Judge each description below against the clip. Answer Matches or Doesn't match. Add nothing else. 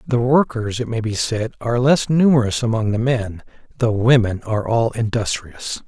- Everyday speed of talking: Matches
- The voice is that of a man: Matches